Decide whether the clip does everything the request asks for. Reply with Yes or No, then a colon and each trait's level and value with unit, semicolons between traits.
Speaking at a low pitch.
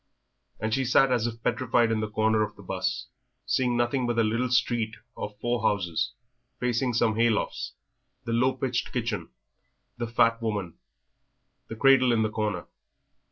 Yes: low, 115 Hz